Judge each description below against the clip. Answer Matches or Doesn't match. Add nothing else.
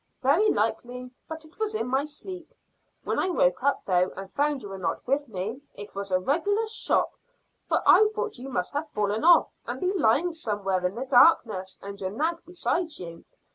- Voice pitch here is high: Matches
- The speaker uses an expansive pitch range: Matches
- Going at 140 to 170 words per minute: Doesn't match